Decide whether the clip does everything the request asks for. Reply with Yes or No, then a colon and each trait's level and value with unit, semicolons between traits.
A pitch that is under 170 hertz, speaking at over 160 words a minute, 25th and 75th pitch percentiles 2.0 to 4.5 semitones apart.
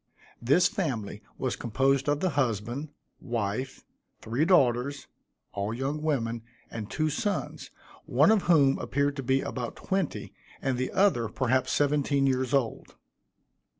No: low, 135 Hz; slow, 135 wpm; average, 3.7 semitones